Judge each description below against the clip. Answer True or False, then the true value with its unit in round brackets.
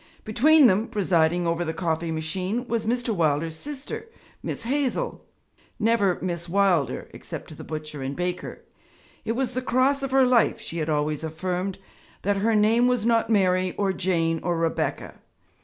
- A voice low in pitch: False (190 Hz)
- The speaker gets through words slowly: False (165 wpm)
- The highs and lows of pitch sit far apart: True (6.0 semitones)